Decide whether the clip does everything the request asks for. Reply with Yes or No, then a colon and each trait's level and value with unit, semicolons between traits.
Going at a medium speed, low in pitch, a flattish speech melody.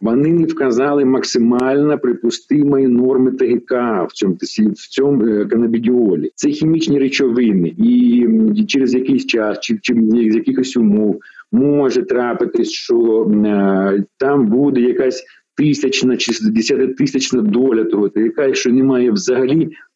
No: average, 125 wpm; low, 130 Hz; average, 3.9 semitones